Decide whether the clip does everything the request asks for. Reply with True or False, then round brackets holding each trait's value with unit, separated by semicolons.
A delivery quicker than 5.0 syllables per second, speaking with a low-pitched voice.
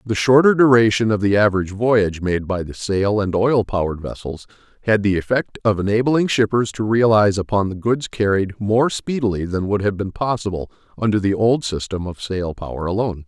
True (5.5 syllables/s; 105 Hz)